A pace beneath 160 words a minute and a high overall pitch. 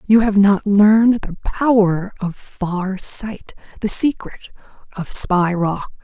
Yes: average, 140 wpm; high, 200 Hz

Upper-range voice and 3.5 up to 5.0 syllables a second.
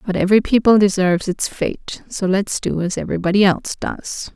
No: high, 195 Hz; 5.6 syllables/s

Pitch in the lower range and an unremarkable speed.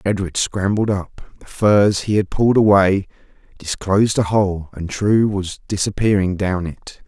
Yes: low, 100 Hz; average, 155 wpm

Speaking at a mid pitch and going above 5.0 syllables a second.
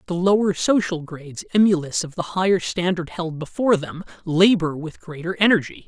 Yes: medium, 175 Hz; 5.4 syllables/s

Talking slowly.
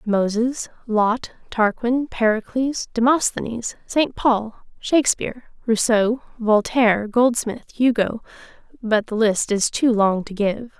Yes: slow, 105 wpm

